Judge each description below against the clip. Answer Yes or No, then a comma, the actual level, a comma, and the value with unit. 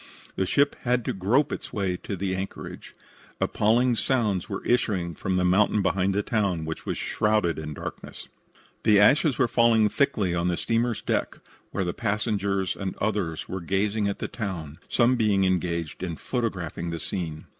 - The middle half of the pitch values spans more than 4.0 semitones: No, average, 3.7 semitones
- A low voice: Yes, low, 100 Hz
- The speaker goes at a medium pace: Yes, average, 175 wpm